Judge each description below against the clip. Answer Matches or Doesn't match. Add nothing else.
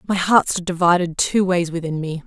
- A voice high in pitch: Doesn't match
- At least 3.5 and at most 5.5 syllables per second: Matches